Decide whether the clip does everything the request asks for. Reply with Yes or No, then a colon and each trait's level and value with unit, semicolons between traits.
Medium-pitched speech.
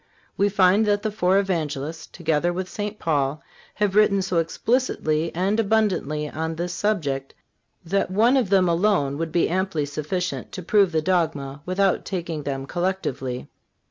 Yes: medium, 180 Hz